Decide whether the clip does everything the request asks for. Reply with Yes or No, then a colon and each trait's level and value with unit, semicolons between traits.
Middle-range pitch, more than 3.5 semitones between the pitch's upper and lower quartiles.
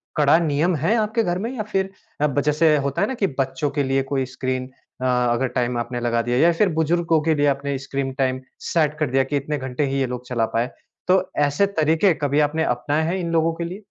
Yes: medium, 145 Hz; average, 4.0 semitones